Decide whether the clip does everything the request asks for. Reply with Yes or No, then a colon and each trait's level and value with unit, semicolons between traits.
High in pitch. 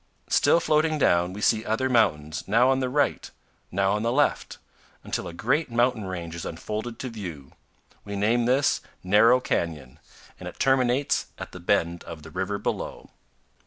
No: low, 110 Hz